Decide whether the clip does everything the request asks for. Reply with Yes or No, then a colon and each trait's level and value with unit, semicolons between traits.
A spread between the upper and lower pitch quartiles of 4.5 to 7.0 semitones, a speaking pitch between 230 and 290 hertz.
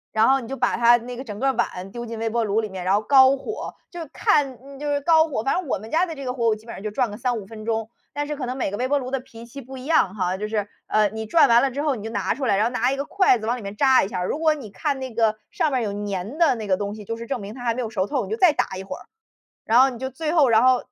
No: average, 4.0 semitones; high, 240 Hz